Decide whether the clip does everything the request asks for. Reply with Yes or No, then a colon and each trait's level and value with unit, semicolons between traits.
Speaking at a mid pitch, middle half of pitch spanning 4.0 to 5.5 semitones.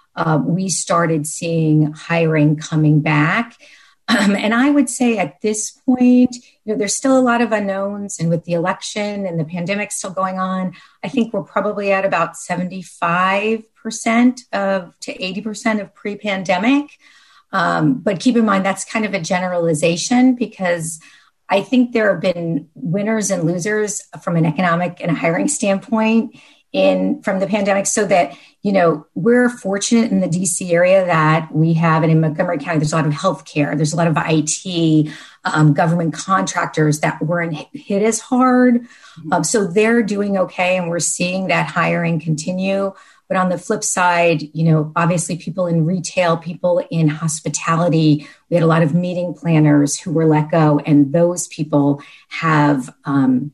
Yes: medium, 180 Hz; average, 4.6 semitones